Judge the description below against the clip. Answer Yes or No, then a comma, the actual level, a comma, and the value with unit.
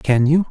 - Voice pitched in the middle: Yes, medium, 150 Hz